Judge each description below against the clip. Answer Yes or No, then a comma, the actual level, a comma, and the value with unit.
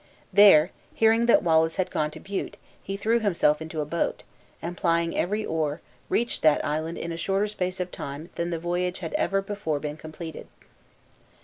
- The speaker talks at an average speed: Yes, average, 185 wpm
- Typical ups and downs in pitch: Yes, average, 3.7 semitones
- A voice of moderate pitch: Yes, medium, 170 Hz